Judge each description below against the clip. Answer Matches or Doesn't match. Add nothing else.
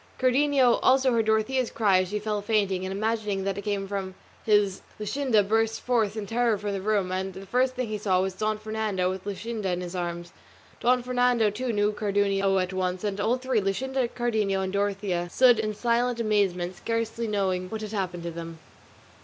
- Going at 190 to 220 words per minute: Matches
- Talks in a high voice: Matches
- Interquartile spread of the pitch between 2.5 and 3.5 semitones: Matches